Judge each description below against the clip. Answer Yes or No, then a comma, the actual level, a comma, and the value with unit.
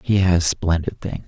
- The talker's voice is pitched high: No, very low, 90 Hz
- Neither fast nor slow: Yes, average, 190 wpm